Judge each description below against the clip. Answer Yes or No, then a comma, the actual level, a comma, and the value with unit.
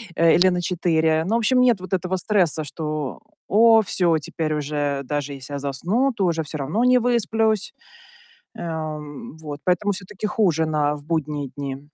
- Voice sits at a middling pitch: Yes, medium, 160 Hz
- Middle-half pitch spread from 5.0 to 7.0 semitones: Yes, average, 5.3 semitones